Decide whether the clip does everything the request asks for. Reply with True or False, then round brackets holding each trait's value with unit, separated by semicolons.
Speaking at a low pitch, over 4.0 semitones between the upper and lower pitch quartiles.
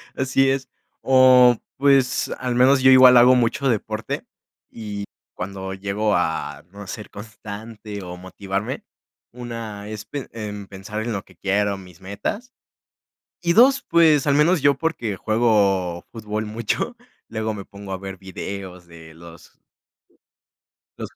True (110 Hz; 4.6 semitones)